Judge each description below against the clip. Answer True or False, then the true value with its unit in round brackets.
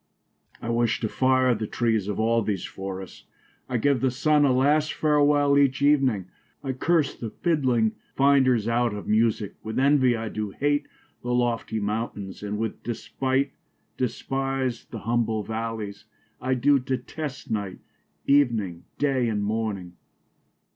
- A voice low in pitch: True (120 Hz)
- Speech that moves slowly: False (145 wpm)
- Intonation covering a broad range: False (3.8 semitones)